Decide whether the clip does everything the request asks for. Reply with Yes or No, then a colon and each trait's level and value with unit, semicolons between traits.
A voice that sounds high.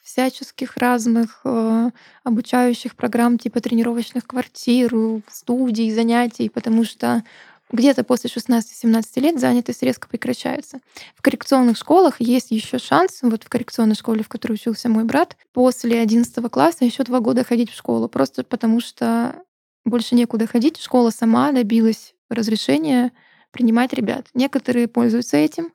Yes: high, 240 Hz